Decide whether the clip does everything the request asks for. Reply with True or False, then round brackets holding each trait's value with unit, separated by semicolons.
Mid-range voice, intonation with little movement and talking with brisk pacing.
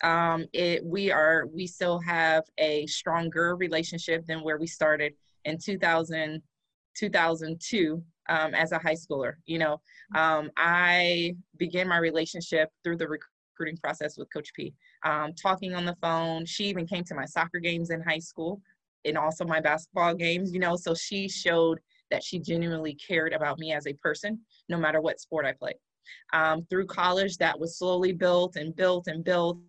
False (165 Hz; 2.0 semitones; 180 wpm)